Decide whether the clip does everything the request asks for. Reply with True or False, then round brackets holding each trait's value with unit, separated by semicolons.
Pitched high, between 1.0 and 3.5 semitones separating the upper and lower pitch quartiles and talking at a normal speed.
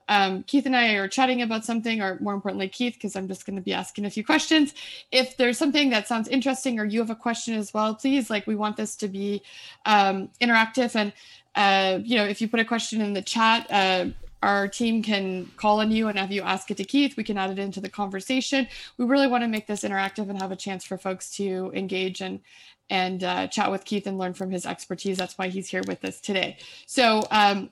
False (210 Hz; 3.2 semitones; 245 wpm)